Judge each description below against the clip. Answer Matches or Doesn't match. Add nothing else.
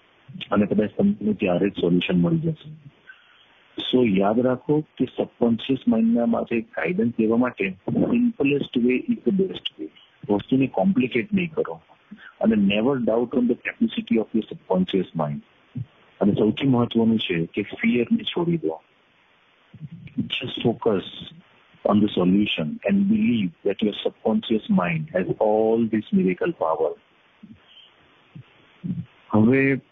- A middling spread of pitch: Doesn't match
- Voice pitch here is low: Matches